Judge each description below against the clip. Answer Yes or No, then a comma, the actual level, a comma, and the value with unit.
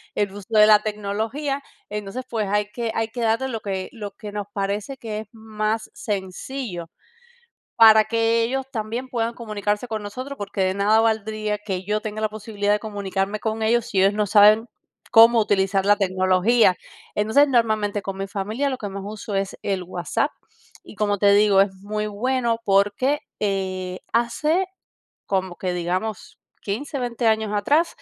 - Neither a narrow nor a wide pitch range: No, narrow, 2.3 semitones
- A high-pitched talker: Yes, high, 210 Hz